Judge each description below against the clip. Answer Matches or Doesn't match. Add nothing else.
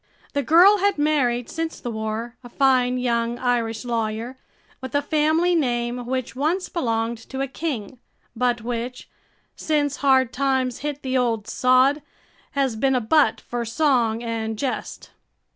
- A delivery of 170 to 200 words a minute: Doesn't match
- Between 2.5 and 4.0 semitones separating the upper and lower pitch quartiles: Matches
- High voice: Matches